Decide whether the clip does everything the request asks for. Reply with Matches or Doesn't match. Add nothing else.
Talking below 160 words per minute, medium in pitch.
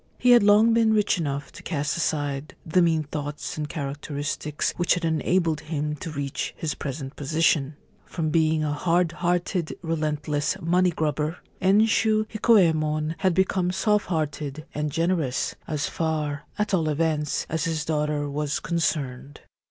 Matches